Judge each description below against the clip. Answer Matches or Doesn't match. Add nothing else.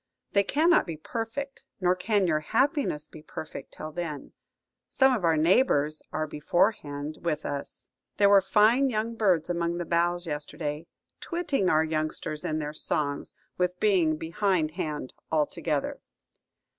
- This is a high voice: Doesn't match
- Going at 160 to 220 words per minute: Doesn't match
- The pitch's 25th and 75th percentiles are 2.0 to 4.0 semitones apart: Doesn't match